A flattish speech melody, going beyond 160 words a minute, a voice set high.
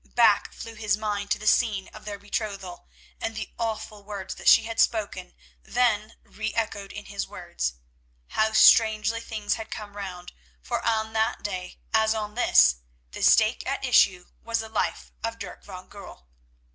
Yes: narrow, 1.9 semitones; average, 170 wpm; high, 215 Hz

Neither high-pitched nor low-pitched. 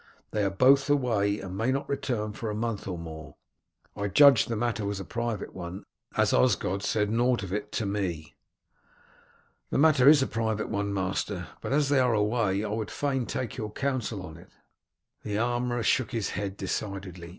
No: low, 105 Hz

